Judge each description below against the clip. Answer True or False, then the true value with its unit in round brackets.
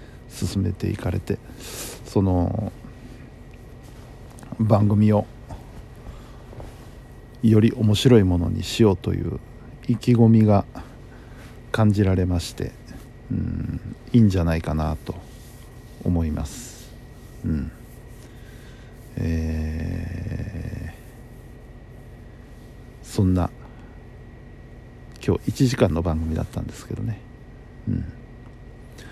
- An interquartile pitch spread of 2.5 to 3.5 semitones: True (3.0 semitones)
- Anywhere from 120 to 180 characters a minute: True (165 characters per minute)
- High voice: False (115 Hz)